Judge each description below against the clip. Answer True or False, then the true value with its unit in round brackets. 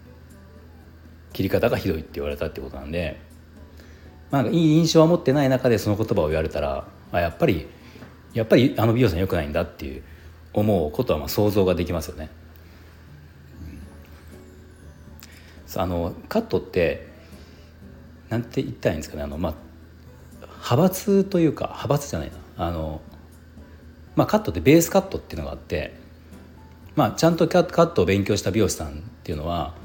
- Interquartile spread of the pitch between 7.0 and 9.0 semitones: False (5.1 semitones)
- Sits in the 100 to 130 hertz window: False (85 Hz)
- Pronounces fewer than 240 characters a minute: False (360 characters per minute)